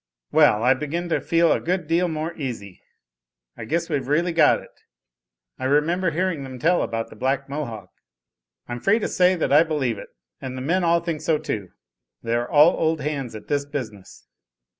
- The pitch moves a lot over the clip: No, average, 4.6 semitones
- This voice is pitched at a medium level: Yes, medium, 150 Hz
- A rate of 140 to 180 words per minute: No, average, 195 wpm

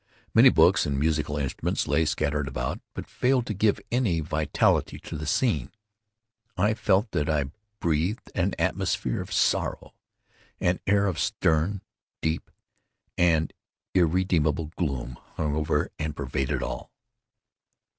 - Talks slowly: Yes, slow, 130 wpm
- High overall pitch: No, very low, 80 Hz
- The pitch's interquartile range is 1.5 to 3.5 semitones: No, average, 4.1 semitones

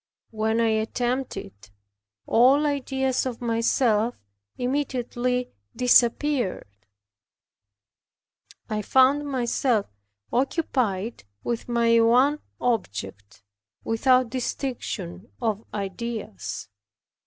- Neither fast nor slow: No, slow, 75 wpm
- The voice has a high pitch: Yes, high, 235 Hz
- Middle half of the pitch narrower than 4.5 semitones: Yes, average, 2.9 semitones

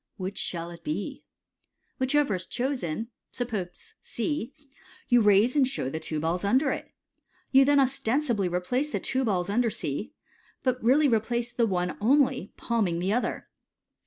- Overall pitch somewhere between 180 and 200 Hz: No, high, 235 Hz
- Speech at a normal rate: Yes, average, 160 wpm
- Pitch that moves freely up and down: Yes, wide, 6.2 semitones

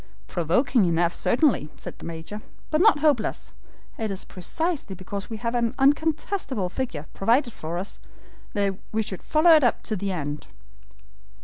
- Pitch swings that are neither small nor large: No, wide, 7.3 semitones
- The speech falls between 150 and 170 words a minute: Yes, average, 155 wpm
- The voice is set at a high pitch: Yes, high, 215 Hz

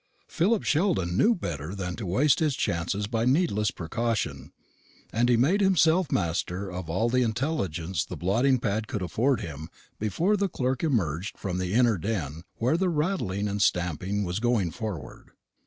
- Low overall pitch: Yes, low, 105 Hz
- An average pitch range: No, wide, 6.9 semitones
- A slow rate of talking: No, average, 165 wpm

